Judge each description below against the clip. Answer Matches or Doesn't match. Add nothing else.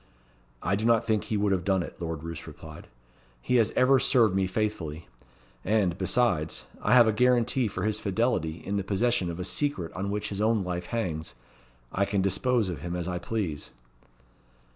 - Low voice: Matches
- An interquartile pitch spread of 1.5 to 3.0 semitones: Doesn't match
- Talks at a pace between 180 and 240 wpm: Matches